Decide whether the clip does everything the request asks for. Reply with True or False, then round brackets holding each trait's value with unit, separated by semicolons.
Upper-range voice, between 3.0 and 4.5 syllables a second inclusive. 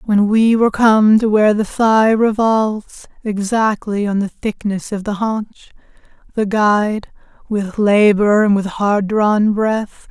True (210 Hz; 4.0 syllables/s)